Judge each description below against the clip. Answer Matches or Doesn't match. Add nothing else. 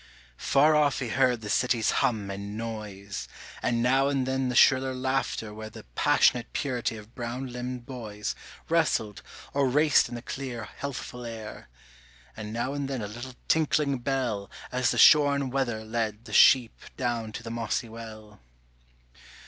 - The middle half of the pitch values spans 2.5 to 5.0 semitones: Matches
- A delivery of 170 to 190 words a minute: Doesn't match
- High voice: Doesn't match